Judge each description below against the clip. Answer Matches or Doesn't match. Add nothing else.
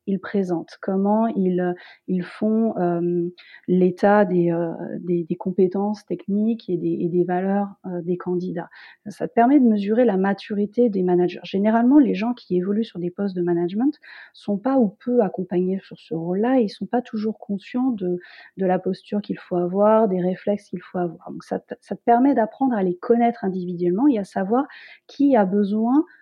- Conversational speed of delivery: Matches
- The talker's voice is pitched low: Doesn't match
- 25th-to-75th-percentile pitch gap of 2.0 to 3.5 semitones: Doesn't match